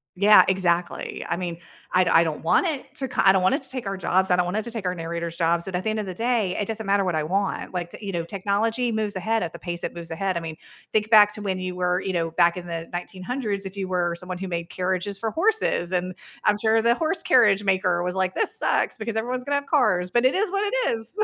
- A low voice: No, high, 190 Hz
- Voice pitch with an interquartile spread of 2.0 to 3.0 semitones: No, average, 3.8 semitones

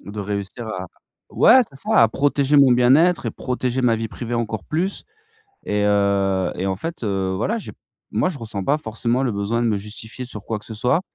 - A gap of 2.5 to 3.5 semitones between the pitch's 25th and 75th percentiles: No, average, 4.4 semitones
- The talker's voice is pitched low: Yes, low, 115 Hz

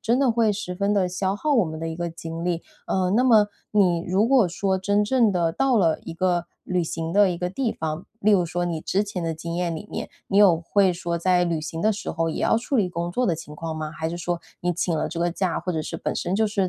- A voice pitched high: No, medium, 180 Hz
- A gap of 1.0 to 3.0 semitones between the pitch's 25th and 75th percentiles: No, average, 3.6 semitones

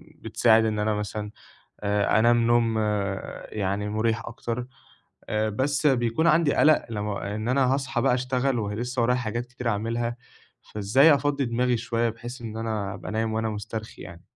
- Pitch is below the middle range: Yes, low, 115 Hz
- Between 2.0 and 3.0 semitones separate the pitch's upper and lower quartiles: Yes, average, 2.7 semitones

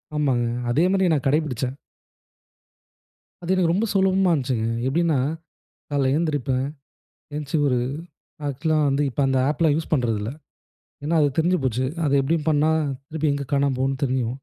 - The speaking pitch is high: No, medium, 145 Hz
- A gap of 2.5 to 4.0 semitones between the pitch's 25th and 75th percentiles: Yes, average, 3.5 semitones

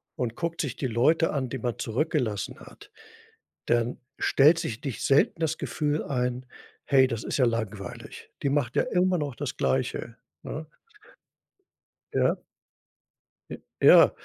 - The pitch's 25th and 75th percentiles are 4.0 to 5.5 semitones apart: Yes, average, 4.5 semitones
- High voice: No, low, 130 Hz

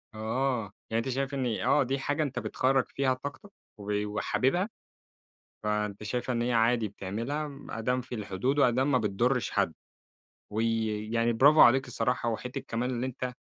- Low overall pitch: Yes, low, 125 Hz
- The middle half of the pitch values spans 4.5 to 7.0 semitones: No, average, 3.1 semitones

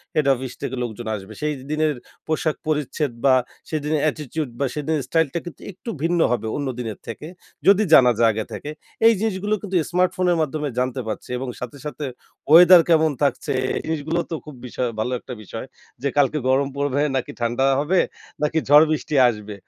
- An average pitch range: Yes, average, 3.9 semitones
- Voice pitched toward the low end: No, medium, 145 Hz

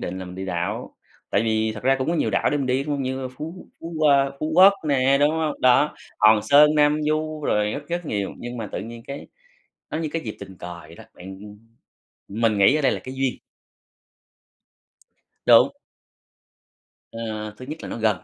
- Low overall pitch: Yes, low, 130 Hz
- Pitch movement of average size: No, wide, 5.8 semitones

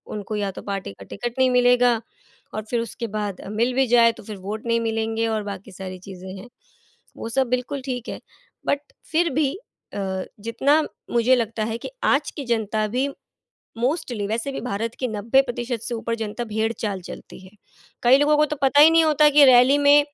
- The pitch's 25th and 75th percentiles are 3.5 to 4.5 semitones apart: Yes, average, 3.8 semitones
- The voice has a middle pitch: No, high, 235 Hz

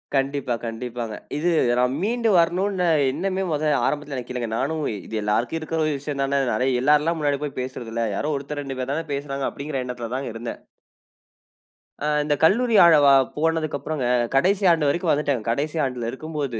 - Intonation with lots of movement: No, average, 4.0 semitones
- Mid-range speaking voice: Yes, medium, 145 Hz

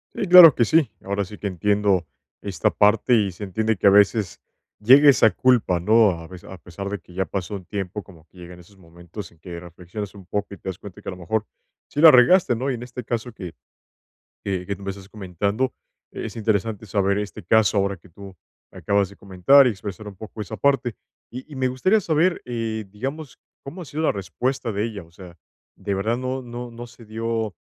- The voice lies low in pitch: Yes, low, 105 Hz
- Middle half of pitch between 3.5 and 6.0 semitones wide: Yes, average, 4.2 semitones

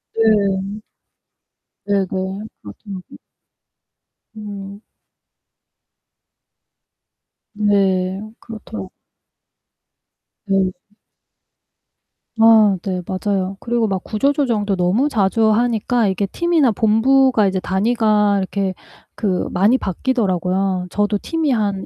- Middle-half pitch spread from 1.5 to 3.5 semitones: Yes, average, 2.8 semitones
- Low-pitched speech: No, high, 205 Hz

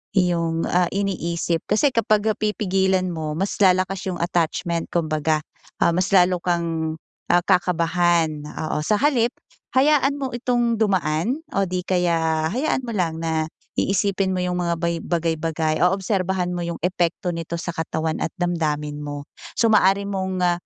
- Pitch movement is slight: No, average, 3.1 semitones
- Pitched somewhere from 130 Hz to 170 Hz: No, medium, 180 Hz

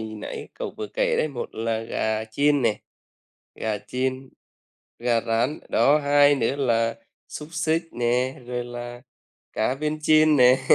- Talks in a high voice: No, low, 125 Hz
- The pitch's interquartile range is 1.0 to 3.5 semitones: No, average, 3.9 semitones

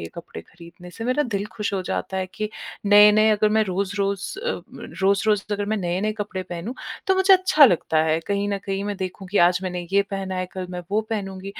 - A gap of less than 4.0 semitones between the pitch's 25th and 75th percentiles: Yes, narrow, 2.4 semitones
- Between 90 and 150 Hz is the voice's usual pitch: No, high, 200 Hz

